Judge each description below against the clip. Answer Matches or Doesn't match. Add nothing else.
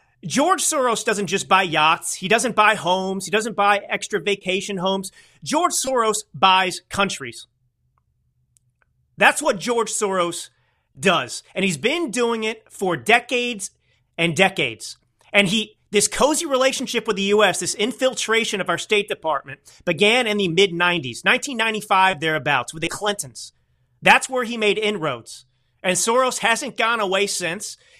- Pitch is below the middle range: Doesn't match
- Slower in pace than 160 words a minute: Matches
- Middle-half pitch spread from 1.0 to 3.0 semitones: Doesn't match